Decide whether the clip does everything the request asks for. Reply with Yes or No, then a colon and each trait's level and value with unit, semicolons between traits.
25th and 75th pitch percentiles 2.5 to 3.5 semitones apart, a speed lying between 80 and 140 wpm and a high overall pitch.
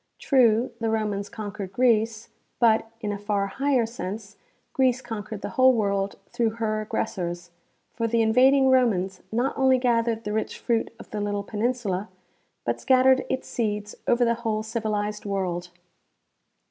No: average, 2.8 semitones; average, 150 wpm; high, 220 Hz